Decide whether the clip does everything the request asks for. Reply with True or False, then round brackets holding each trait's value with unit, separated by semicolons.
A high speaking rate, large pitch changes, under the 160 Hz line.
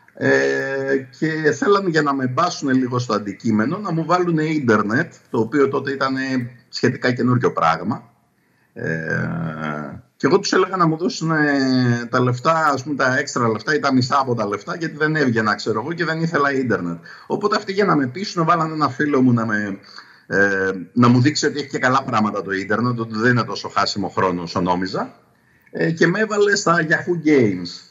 True (190 wpm; 6.0 semitones; 135 Hz)